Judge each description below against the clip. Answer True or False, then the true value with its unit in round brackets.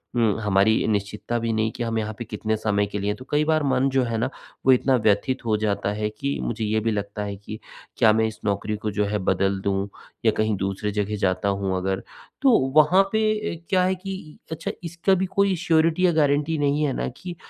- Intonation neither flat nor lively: False (6.3 semitones)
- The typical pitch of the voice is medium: False (110 Hz)